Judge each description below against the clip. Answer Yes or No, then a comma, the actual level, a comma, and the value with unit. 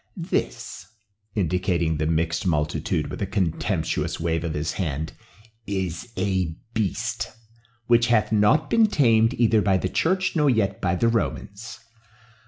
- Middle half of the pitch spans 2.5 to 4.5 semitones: No, wide, 5.5 semitones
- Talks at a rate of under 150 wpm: Yes, average, 140 wpm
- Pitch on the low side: Yes, low, 100 Hz